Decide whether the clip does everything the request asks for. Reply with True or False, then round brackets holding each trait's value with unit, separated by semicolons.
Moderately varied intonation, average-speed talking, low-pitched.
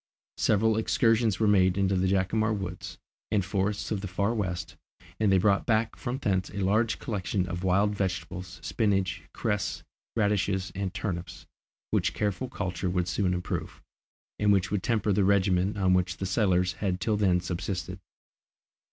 False (2.3 semitones; 160 wpm; 95 Hz)